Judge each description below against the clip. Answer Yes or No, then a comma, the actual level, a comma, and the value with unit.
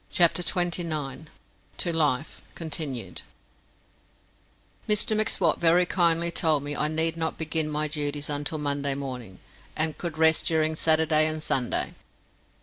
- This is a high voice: No, medium, 155 Hz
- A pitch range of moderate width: No, narrow, 2.1 semitones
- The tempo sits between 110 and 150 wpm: Yes, slow, 135 wpm